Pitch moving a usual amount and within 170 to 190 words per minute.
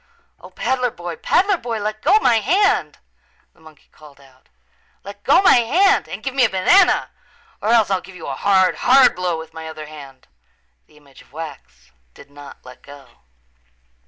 No: wide, 8.8 semitones; average, 185 wpm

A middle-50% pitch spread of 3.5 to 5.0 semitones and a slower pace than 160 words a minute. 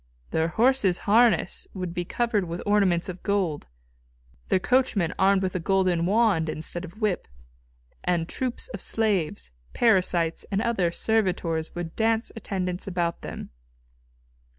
Yes: average, 4.0 semitones; slow, 135 wpm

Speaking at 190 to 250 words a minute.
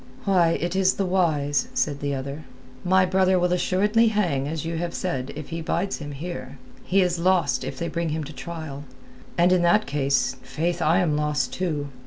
Yes: average, 200 wpm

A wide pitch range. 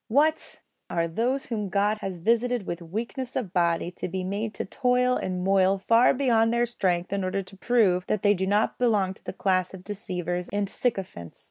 No: average, 4.1 semitones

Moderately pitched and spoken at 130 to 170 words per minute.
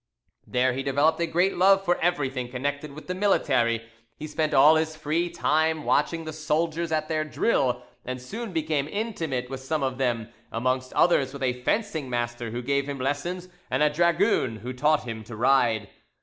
No: medium, 145 Hz; average, 185 wpm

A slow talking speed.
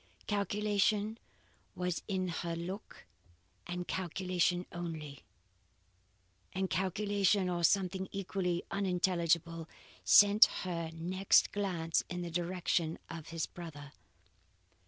Yes: slow, 95 wpm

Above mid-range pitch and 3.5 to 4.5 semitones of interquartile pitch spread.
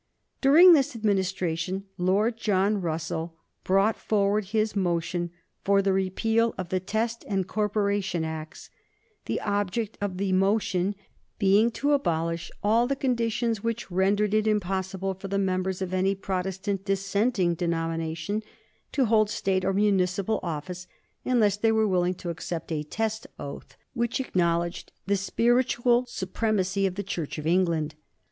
No: high, 195 Hz; average, 3.1 semitones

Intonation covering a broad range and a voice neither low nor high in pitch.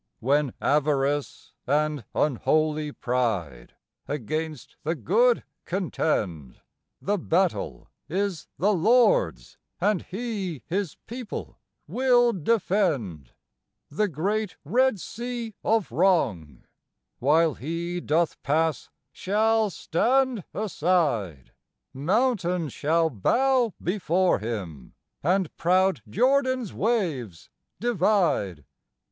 Yes: wide, 7.0 semitones; medium, 170 Hz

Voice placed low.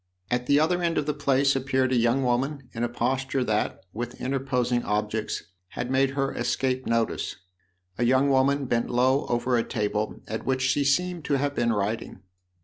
Yes: low, 130 Hz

